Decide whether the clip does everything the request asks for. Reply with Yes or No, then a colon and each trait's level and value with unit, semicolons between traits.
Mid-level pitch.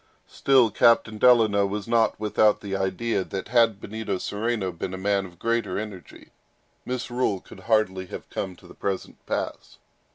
No: low, 105 Hz